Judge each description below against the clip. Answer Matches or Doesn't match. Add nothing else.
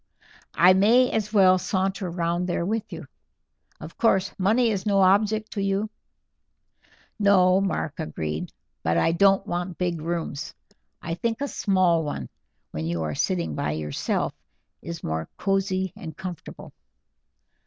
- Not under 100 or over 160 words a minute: Matches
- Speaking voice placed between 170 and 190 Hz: Matches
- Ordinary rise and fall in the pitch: Matches